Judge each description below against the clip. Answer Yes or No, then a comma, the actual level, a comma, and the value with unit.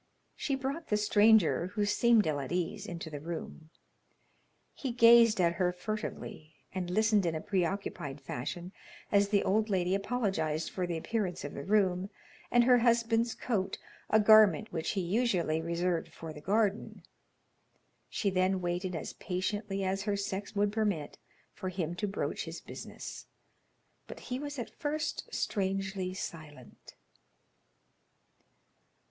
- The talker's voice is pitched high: Yes, high, 195 Hz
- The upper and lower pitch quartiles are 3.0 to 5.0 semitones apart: Yes, average, 3.8 semitones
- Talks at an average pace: Yes, average, 145 wpm